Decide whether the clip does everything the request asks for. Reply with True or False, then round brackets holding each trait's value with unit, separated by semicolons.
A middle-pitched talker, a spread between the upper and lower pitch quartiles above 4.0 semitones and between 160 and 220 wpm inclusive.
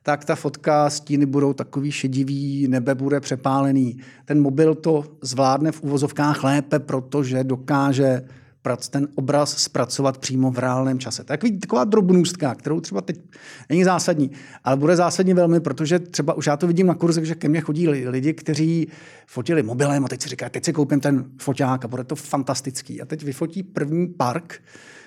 False (145 Hz; 2.9 semitones; 170 wpm)